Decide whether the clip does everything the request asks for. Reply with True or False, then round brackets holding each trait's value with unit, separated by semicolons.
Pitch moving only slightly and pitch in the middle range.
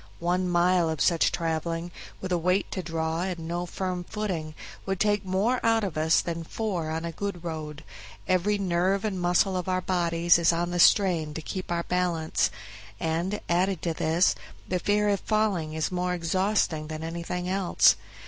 True (2.3 semitones; 175 Hz)